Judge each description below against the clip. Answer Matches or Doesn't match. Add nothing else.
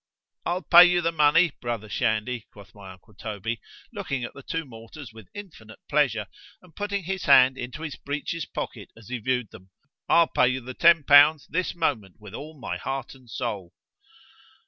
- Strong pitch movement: Matches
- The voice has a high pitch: Doesn't match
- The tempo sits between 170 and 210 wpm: Matches